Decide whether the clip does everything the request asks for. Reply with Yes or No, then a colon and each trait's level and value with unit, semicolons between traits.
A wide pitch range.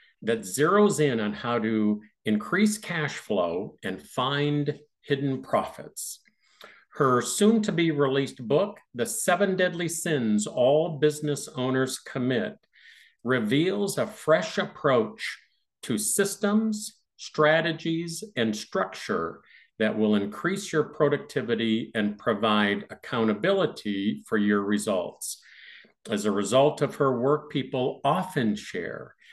Yes: wide, 7.4 semitones